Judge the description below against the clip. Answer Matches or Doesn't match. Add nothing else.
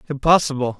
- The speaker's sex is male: Matches